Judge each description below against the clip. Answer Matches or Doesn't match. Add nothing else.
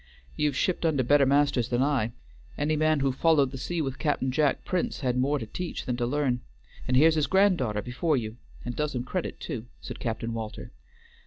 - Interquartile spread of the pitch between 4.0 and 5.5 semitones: Doesn't match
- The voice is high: Doesn't match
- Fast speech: Matches